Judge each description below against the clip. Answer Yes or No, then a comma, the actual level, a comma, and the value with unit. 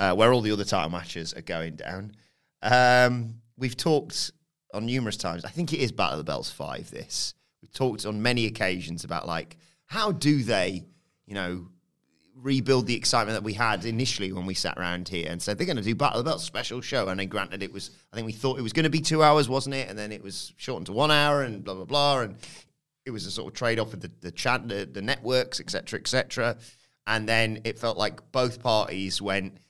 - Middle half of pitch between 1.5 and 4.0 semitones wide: No, average, 5.2 semitones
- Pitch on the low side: Yes, low, 115 Hz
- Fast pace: Yes, fast, 240 wpm